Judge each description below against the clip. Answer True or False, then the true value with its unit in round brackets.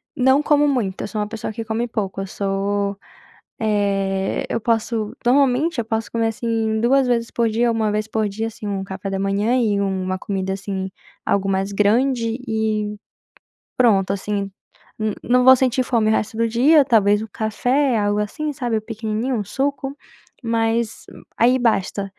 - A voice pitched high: True (220 Hz)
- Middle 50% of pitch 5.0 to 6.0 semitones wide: False (3.0 semitones)